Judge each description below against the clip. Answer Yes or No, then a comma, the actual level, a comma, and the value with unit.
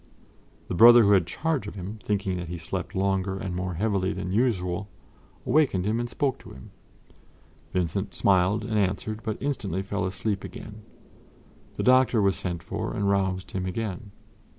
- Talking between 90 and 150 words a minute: No, average, 170 wpm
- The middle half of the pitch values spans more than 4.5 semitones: No, average, 2.8 semitones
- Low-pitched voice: Yes, low, 100 Hz